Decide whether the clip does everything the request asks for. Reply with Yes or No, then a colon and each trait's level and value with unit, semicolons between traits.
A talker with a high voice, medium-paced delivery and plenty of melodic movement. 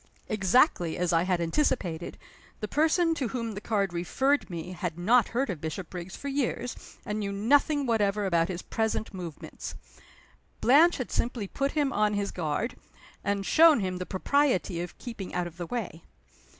Yes: high, 205 Hz; average, 170 wpm; wide, 6.0 semitones